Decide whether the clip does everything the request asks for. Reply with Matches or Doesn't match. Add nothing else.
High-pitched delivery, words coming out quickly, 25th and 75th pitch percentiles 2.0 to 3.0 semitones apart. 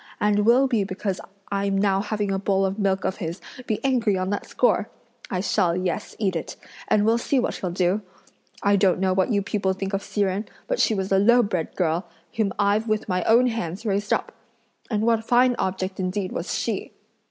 Matches